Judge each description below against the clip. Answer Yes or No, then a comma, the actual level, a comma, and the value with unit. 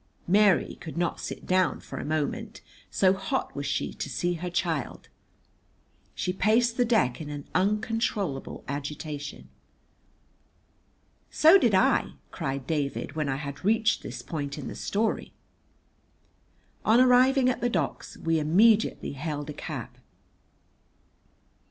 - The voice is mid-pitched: Yes, medium, 175 Hz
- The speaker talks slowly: Yes, slow, 130 wpm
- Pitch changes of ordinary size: No, wide, 7.0 semitones